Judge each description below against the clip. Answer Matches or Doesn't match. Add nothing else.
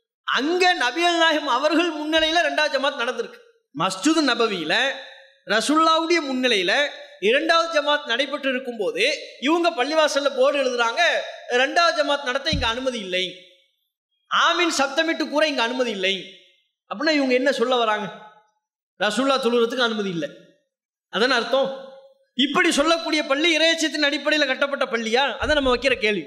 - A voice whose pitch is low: Doesn't match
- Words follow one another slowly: Matches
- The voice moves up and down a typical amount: Matches